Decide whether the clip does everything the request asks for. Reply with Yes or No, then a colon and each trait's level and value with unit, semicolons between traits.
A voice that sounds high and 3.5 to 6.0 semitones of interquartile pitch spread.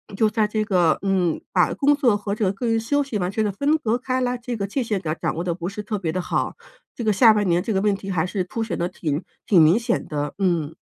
Yes: high, 200 Hz; average, 4.2 semitones